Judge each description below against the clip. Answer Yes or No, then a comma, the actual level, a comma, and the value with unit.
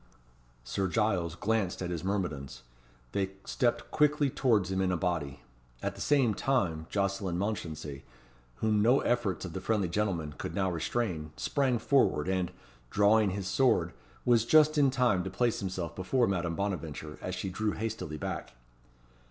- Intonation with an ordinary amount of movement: Yes, average, 4.6 semitones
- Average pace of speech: Yes, average, 160 wpm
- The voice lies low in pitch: Yes, very low, 95 Hz